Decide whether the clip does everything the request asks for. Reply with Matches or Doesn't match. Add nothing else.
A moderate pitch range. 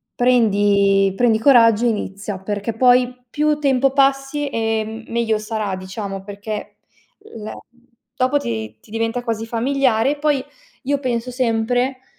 Matches